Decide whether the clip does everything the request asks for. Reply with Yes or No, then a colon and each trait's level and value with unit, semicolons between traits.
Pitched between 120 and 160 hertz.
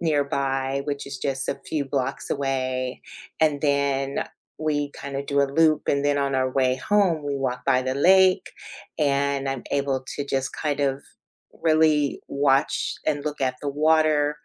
Yes: medium, 140 Hz